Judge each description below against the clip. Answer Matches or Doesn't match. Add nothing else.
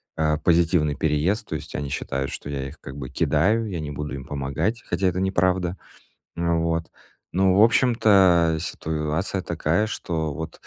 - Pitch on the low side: Matches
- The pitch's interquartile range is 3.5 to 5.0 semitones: Matches